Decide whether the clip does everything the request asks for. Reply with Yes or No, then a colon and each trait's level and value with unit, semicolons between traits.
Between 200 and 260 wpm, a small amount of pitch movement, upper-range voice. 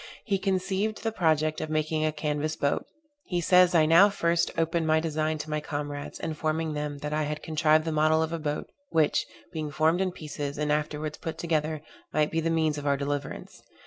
No: fast, 205 wpm; narrow, 1.5 semitones; medium, 155 Hz